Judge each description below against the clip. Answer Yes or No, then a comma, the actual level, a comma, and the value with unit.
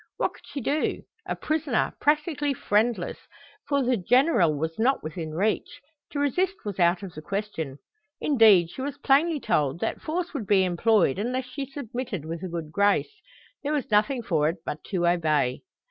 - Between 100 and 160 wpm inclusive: No, average, 175 wpm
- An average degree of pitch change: No, wide, 8.4 semitones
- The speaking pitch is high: Yes, high, 215 Hz